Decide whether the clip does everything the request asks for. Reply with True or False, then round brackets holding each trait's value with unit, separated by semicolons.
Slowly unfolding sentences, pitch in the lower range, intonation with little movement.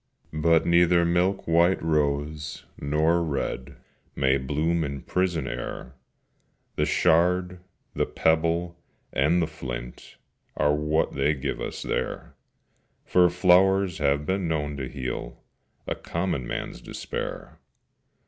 False (120 wpm; 80 Hz; 3.4 semitones)